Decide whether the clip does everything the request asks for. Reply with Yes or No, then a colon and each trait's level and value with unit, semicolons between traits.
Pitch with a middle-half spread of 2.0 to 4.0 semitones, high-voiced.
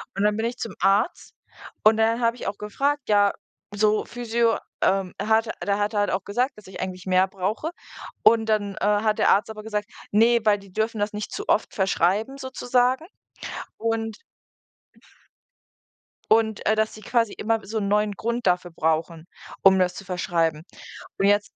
Yes: narrow, 2.5 semitones; high, 210 Hz